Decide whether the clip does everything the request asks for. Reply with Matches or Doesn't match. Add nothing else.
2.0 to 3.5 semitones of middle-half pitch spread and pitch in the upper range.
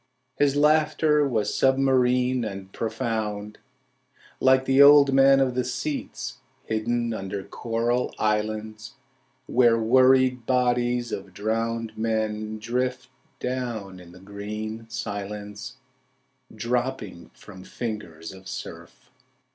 Doesn't match